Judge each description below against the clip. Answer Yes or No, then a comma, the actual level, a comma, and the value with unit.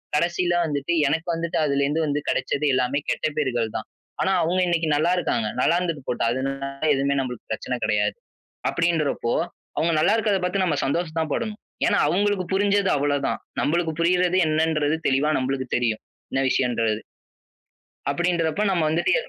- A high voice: No, medium, 155 Hz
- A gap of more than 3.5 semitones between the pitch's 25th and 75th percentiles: Yes, average, 4.1 semitones